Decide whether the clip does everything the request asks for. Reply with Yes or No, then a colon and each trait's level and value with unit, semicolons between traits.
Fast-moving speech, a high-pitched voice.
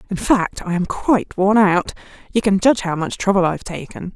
Yes: fast, 230 wpm; high, 195 Hz